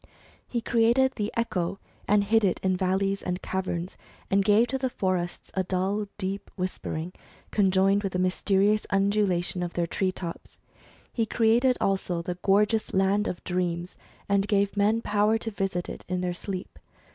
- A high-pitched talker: Yes, high, 195 Hz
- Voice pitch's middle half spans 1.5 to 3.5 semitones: Yes, narrow, 2.4 semitones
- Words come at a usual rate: Yes, average, 170 wpm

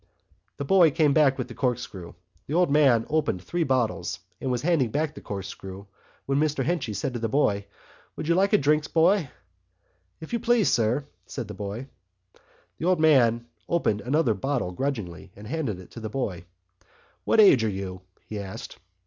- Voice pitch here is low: Yes, low, 130 Hz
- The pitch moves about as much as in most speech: No, wide, 6.7 semitones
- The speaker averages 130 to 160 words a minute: No, average, 185 wpm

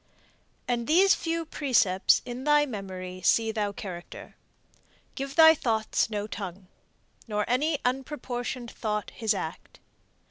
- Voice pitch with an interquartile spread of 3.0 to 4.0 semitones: No, average, 5.2 semitones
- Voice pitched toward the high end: Yes, high, 230 Hz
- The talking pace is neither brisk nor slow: No, slow, 120 wpm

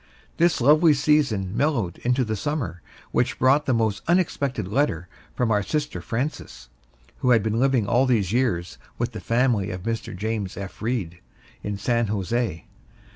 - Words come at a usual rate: Yes, average, 160 wpm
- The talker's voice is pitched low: Yes, low, 115 Hz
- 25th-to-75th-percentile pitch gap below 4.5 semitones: No, average, 5.2 semitones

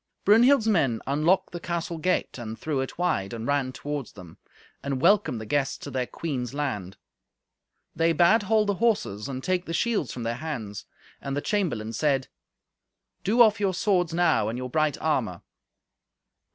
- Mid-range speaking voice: Yes, medium, 145 Hz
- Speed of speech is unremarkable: Yes, average, 170 wpm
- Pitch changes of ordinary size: No, wide, 6.5 semitones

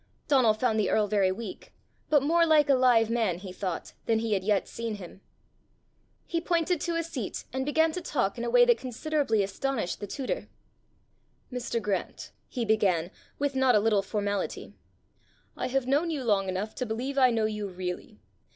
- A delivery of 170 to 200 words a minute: Yes, average, 190 wpm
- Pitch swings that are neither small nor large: Yes, average, 4.9 semitones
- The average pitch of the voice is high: Yes, high, 230 Hz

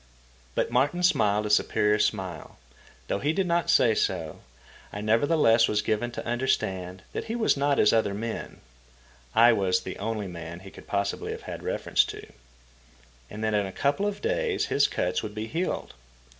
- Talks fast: No, average, 180 wpm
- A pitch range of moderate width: No, wide, 6.2 semitones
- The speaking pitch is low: Yes, low, 110 Hz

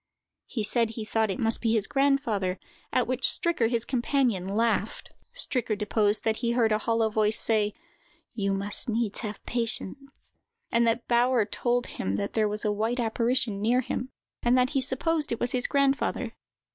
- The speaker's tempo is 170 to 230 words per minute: Yes, average, 180 wpm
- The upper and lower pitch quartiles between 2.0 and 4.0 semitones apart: Yes, average, 2.8 semitones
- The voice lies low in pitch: No, high, 230 Hz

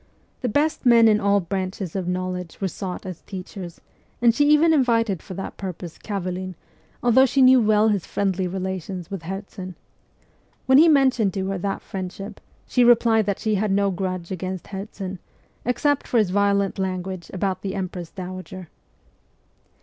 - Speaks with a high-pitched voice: Yes, high, 195 Hz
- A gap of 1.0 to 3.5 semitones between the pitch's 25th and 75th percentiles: Yes, average, 3.1 semitones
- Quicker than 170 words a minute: No, average, 165 wpm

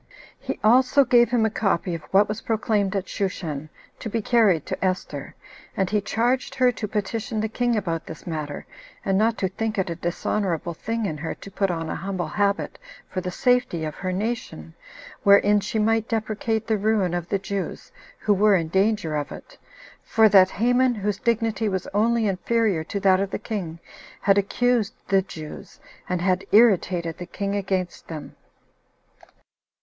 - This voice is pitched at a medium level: No, high, 200 Hz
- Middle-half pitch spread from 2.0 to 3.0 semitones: No, average, 3.4 semitones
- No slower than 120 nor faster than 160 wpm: No, average, 180 wpm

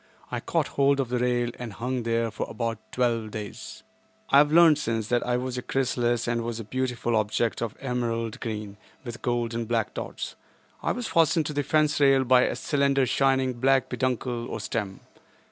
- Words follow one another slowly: No, average, 195 wpm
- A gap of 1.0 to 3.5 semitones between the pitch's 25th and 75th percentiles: Yes, narrow, 2.5 semitones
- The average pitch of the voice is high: No, low, 120 Hz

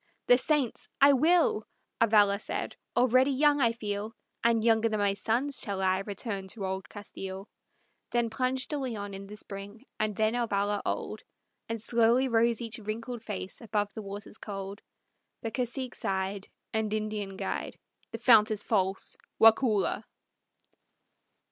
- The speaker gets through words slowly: No, average, 150 wpm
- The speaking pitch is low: No, high, 220 Hz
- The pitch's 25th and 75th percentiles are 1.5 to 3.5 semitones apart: Yes, average, 2.8 semitones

